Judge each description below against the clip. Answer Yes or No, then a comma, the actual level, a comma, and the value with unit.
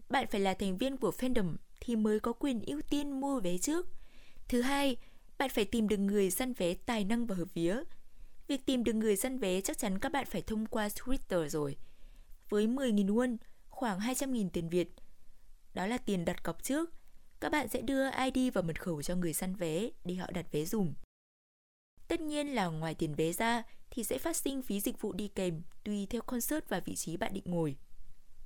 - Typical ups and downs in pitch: No, wide, 6.4 semitones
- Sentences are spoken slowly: No, average, 210 wpm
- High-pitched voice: Yes, high, 220 Hz